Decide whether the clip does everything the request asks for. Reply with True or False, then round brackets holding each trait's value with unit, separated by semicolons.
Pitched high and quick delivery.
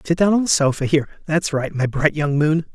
False (155 Hz; 265 wpm)